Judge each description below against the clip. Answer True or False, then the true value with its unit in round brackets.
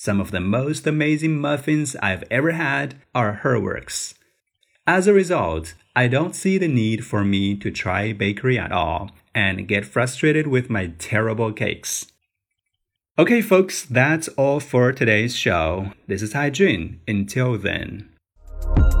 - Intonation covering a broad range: True (6.6 semitones)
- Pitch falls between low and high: False (110 Hz)